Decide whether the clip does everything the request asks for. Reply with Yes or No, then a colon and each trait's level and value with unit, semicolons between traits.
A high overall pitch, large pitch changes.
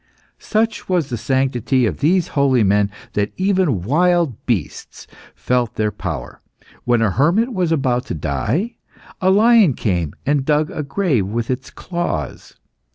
No: low, 135 Hz; wide, 7.9 semitones